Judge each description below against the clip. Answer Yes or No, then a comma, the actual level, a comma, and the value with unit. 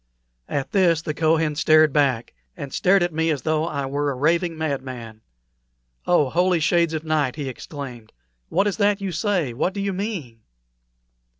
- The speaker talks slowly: No, average, 175 wpm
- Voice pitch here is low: No, medium, 155 Hz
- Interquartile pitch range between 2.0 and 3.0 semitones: No, average, 4.0 semitones